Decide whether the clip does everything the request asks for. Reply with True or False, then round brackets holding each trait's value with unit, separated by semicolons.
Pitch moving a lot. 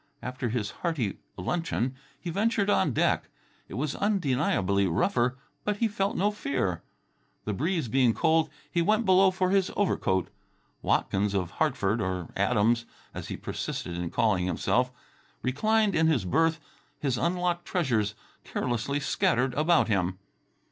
True (9.0 semitones)